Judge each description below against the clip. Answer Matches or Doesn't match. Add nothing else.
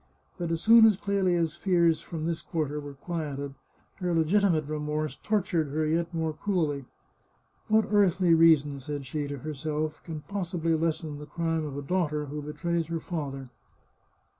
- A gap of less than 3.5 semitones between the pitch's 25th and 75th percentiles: Matches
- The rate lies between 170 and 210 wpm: Matches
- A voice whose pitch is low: Doesn't match